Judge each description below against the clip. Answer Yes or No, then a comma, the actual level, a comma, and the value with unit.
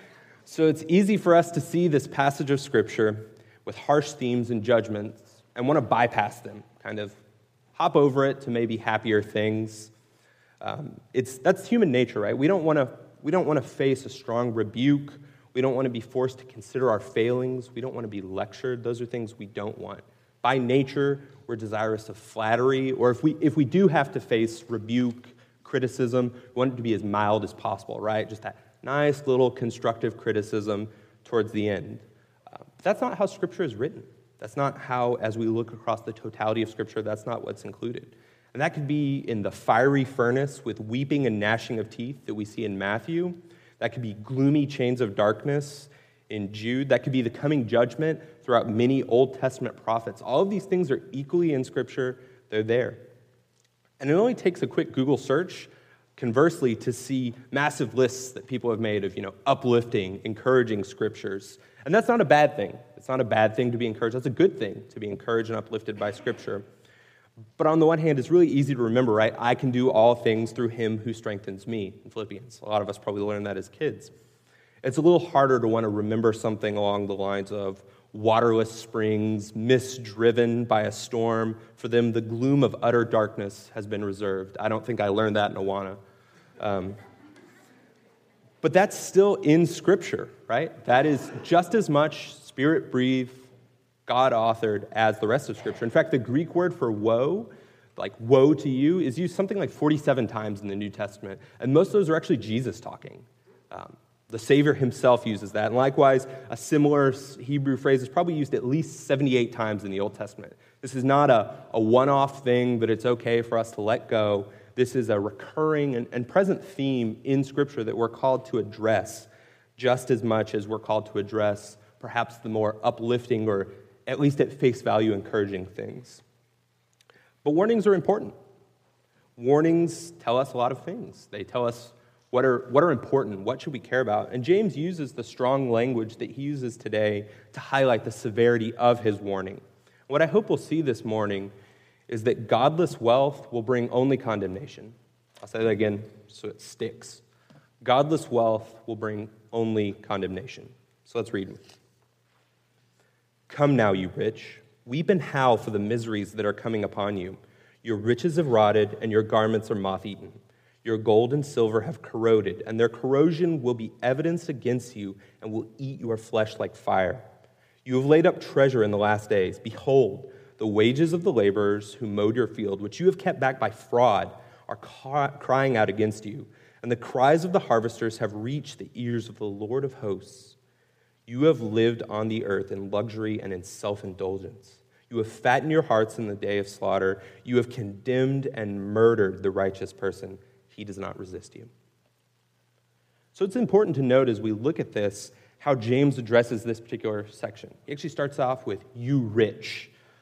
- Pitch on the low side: Yes, low, 120 Hz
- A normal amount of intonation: Yes, average, 4.1 semitones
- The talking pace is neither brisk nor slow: Yes, average, 190 wpm